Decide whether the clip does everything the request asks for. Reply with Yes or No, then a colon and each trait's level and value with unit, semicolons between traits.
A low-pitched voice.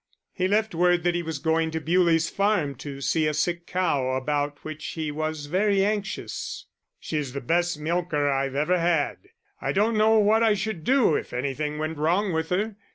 No: medium, 165 Hz